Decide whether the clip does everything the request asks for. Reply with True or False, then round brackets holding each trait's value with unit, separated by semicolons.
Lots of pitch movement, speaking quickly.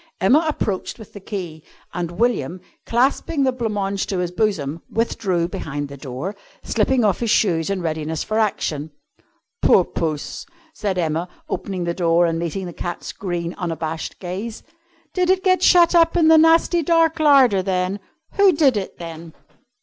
False (6.7 semitones; 165 wpm)